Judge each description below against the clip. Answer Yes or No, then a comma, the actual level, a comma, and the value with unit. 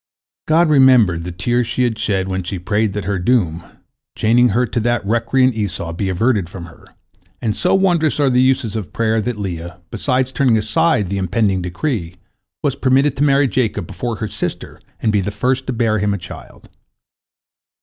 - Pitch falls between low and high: No, low, 110 Hz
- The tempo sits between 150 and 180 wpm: No, average, 190 wpm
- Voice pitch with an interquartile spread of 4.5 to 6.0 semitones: Yes, average, 5.0 semitones